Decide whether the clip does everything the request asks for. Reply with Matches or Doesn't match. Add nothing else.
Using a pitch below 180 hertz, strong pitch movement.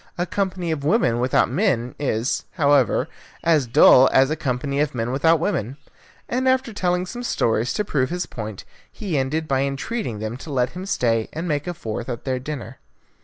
Matches